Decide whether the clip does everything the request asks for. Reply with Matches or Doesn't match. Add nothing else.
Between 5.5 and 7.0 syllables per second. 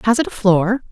Matches